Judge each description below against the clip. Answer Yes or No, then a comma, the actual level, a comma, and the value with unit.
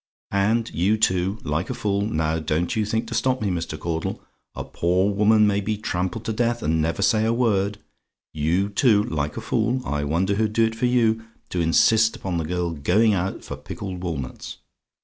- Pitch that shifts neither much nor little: Yes, average, 4.7 semitones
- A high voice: No, low, 100 Hz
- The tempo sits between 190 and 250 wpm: Yes, average, 200 wpm